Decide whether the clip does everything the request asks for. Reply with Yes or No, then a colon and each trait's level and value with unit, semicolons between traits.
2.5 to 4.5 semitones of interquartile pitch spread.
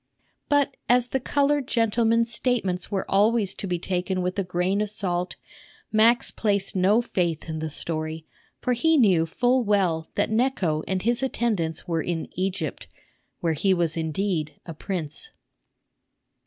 No: wide, 5.4 semitones